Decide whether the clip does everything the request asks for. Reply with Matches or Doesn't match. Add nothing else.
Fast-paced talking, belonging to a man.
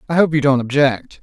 Matches